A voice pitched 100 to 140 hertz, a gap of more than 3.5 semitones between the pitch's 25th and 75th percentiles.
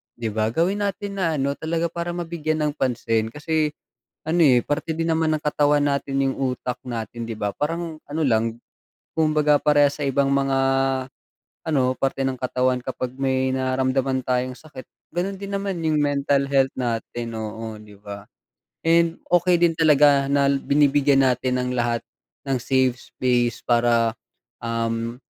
Yes: low, 135 Hz; average, 4.0 semitones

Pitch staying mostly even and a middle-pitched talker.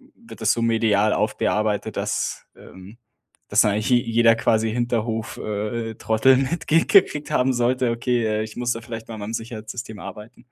No: narrow, 2.1 semitones; low, 115 Hz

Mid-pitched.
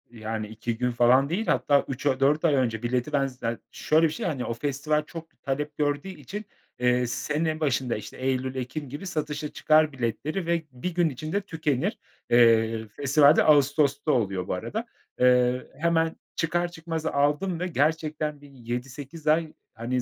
Yes: medium, 145 Hz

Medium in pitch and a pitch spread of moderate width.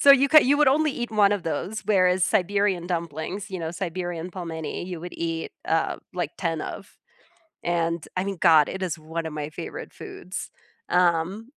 Yes: medium, 180 Hz; average, 3.6 semitones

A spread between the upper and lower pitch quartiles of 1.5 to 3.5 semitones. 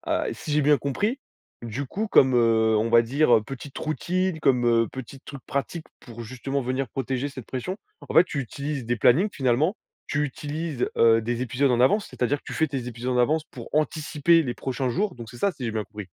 No: average, 4.0 semitones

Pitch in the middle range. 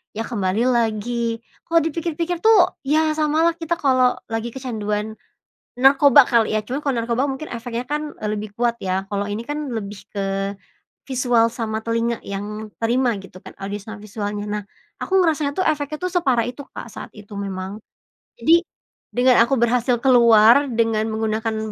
No: high, 235 Hz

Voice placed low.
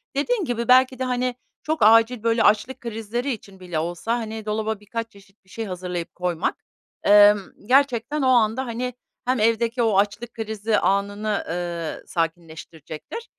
No: high, 220 Hz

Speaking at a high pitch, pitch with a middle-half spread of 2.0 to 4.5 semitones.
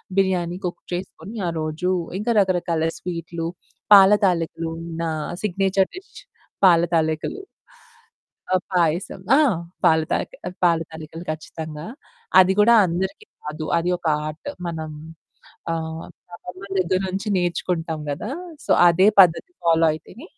No: medium, 175 Hz; average, 2.7 semitones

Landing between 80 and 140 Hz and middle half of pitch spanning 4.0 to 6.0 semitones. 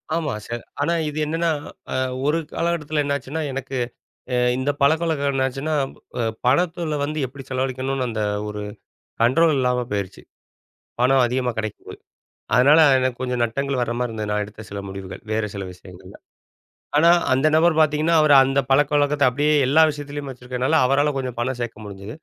No: low, 135 Hz; average, 3.6 semitones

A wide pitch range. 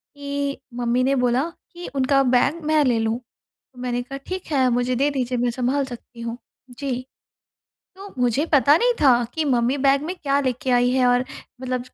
No: narrow, 2.4 semitones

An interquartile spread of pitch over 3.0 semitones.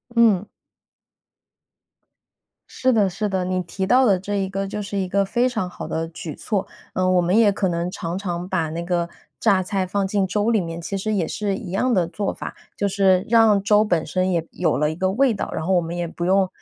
No: narrow, 2.6 semitones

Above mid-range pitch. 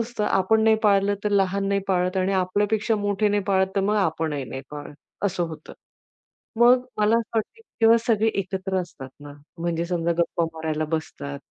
Yes: high, 195 Hz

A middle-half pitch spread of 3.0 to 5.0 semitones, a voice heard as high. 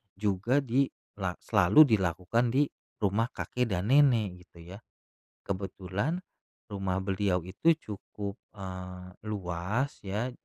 No: average, 4.3 semitones; low, 100 Hz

